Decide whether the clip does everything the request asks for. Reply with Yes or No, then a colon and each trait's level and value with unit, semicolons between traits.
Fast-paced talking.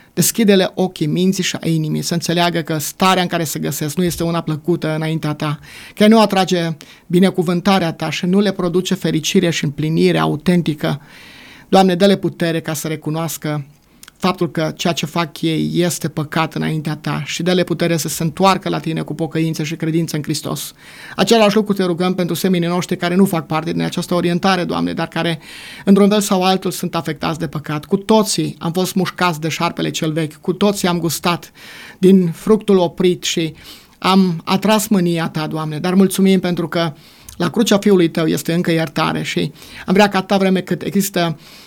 Yes: fast, 185 wpm